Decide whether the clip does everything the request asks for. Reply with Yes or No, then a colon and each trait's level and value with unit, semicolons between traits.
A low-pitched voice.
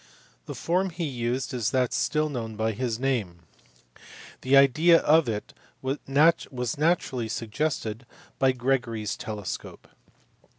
Yes: low, 130 Hz